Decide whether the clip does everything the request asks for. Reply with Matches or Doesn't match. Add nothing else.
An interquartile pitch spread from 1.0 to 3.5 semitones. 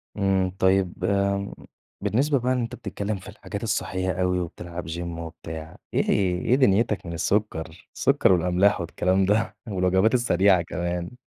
Matches